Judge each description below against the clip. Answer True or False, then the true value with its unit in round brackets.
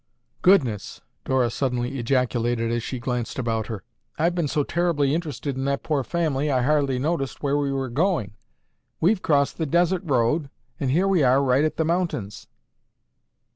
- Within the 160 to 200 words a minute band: True (170 wpm)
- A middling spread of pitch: True (4.4 semitones)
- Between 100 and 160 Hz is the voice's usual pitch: True (140 Hz)